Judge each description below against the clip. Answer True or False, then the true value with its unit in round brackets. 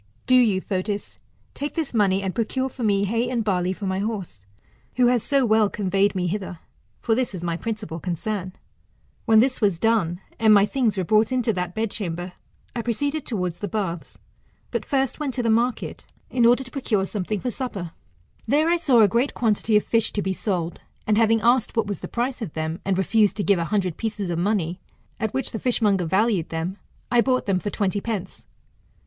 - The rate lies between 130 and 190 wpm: False (205 wpm)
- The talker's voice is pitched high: True (210 Hz)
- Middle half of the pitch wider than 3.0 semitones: True (3.9 semitones)